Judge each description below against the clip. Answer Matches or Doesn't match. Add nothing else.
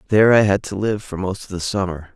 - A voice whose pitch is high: Doesn't match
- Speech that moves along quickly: Matches